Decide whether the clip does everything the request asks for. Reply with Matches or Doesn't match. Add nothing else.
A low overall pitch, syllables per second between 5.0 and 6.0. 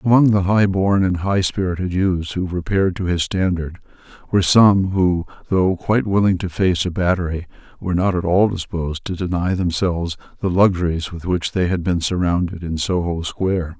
Matches